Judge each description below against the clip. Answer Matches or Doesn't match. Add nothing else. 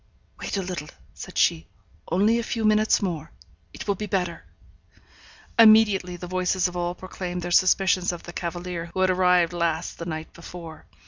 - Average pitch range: Doesn't match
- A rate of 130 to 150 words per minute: Doesn't match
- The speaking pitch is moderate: Matches